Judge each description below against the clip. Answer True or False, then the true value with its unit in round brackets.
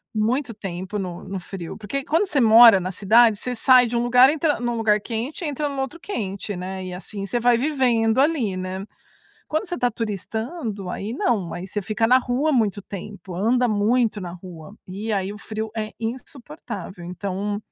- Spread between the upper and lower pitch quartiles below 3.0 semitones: False (4.2 semitones)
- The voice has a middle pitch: False (220 Hz)